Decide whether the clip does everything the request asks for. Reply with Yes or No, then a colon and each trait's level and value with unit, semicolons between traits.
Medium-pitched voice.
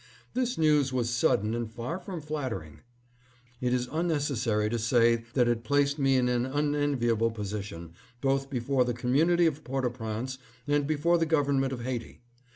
No: low, 130 Hz